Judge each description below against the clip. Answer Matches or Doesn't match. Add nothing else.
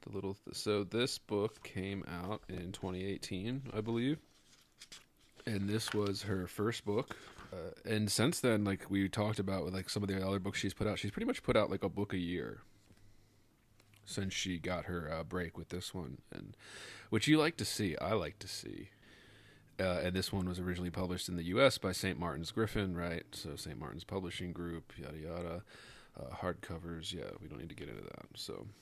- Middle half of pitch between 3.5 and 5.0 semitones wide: Doesn't match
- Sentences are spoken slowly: Doesn't match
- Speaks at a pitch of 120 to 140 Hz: Doesn't match